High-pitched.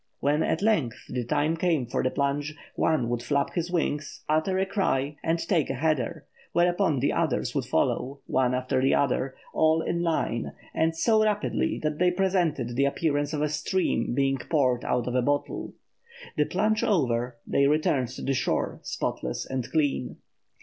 No: medium, 145 Hz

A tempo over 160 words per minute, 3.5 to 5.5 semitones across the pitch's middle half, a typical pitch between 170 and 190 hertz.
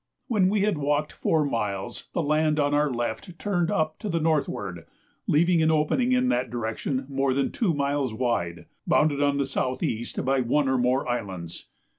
No: average, 185 wpm; average, 4.5 semitones; medium, 140 Hz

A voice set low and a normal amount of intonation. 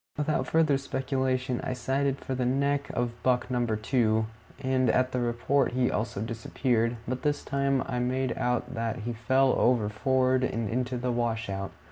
No: low, 125 Hz; narrow, 2.1 semitones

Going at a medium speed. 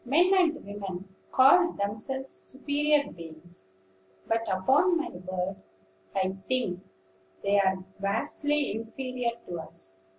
No: slow, 110 wpm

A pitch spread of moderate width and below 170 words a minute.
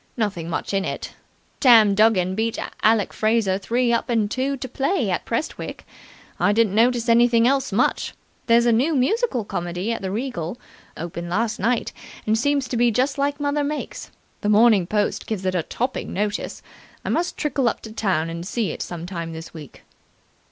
No: average, 4.5 semitones; average, 185 wpm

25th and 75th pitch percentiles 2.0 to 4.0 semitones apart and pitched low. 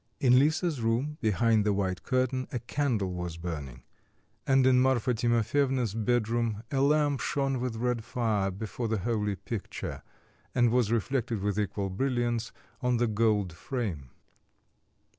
Yes: average, 3.7 semitones; low, 115 Hz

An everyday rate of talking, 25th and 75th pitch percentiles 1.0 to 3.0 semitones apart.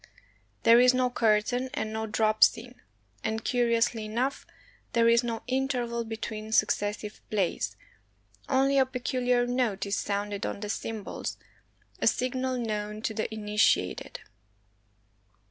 No: slow, 130 wpm; average, 2.7 semitones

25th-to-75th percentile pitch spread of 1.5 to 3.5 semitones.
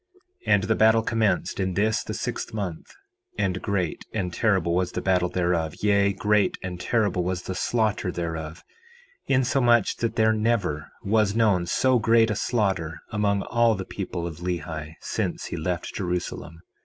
No: average, 3.9 semitones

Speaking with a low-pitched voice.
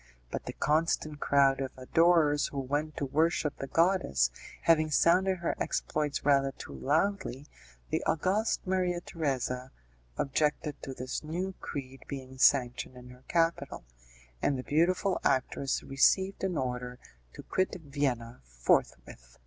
No: medium, 145 Hz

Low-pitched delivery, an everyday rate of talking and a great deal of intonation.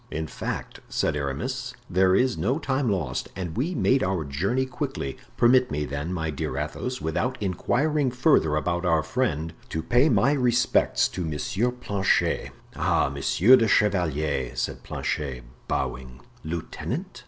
Yes: very low, 95 Hz; average, 145 wpm; wide, 8.6 semitones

